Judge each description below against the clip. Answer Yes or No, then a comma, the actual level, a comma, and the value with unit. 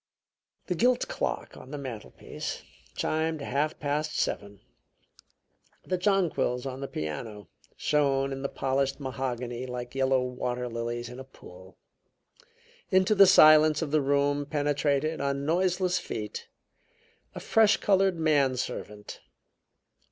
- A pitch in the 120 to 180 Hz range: Yes, medium, 140 Hz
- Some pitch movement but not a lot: Yes, average, 4.0 semitones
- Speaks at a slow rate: Yes, slow, 125 wpm